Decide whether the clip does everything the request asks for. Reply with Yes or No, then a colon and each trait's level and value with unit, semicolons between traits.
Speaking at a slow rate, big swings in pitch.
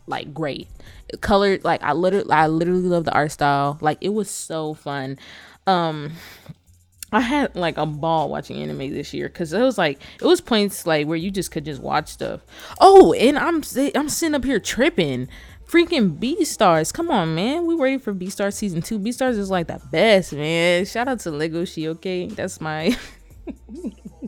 No: average, 195 wpm; wide, 7.1 semitones